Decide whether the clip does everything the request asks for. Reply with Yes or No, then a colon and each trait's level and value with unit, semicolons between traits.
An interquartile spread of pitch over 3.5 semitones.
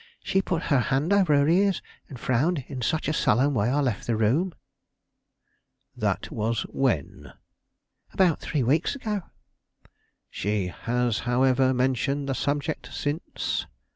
Yes: average, 4.5 semitones